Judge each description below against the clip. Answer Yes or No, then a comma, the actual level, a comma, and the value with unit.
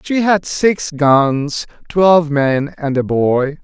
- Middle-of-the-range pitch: Yes, medium, 155 Hz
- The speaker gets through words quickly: No, average, 150 wpm